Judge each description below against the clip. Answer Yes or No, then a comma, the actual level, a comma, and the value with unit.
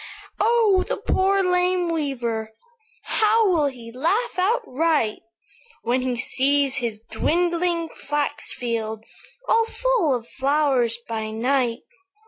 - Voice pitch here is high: Yes, very high, 285 Hz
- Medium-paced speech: No, slow, 110 wpm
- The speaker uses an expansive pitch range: Yes, wide, 7.1 semitones